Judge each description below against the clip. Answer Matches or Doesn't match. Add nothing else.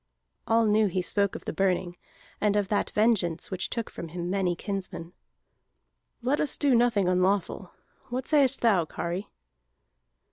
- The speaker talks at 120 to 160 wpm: Matches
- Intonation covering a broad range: Doesn't match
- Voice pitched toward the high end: Matches